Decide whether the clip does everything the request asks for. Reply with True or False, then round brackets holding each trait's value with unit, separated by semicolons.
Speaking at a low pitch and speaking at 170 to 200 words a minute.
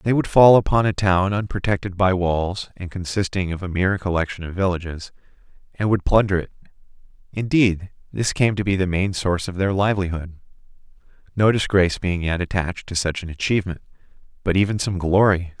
True (95 Hz; 175 wpm)